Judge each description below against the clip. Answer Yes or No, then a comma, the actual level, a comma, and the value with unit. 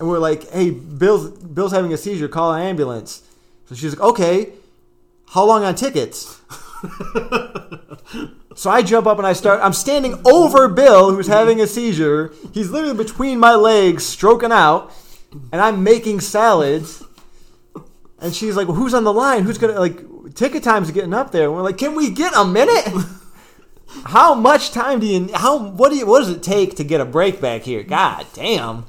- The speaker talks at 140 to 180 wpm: No, average, 190 wpm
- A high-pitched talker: Yes, high, 200 Hz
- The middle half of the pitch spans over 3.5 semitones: Yes, average, 5.3 semitones